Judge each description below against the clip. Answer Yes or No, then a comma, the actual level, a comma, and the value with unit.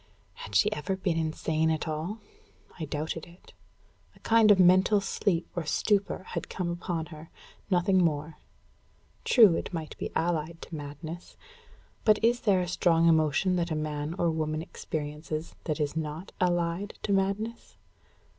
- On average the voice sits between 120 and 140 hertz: No, medium, 170 Hz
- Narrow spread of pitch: No, average, 3.1 semitones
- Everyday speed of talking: Yes, average, 155 wpm